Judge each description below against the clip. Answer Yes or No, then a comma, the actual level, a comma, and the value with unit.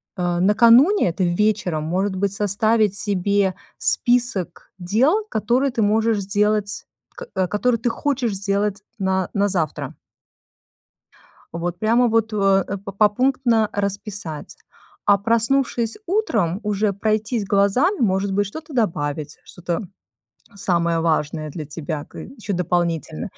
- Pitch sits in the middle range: No, high, 205 Hz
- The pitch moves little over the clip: No, average, 4.0 semitones